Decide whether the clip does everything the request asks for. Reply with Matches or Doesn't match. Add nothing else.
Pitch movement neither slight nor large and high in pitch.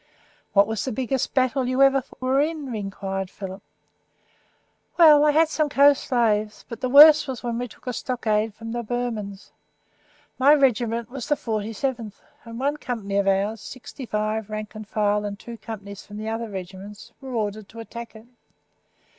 Matches